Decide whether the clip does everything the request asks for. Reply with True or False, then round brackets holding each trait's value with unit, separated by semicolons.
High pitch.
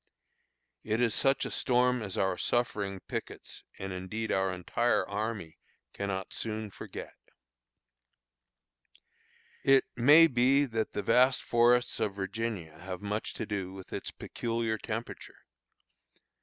False (110 Hz)